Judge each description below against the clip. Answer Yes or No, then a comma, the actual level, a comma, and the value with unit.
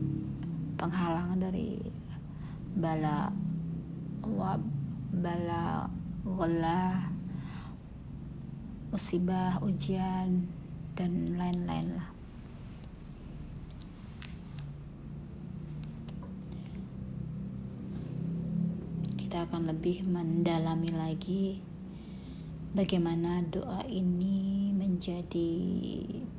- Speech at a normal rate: No, slow, 45 wpm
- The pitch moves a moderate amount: No, narrow, 2.3 semitones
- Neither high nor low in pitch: Yes, medium, 175 Hz